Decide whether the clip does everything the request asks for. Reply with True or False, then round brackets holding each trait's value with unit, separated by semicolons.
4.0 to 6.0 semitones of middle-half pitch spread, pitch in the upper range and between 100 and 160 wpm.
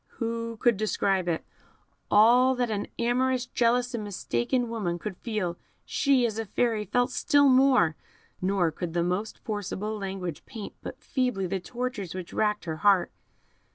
True (4.7 semitones; 215 Hz; 155 wpm)